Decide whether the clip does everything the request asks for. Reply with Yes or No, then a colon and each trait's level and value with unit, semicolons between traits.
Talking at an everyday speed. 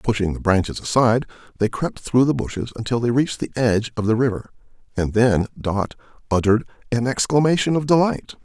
Yes: average, 180 wpm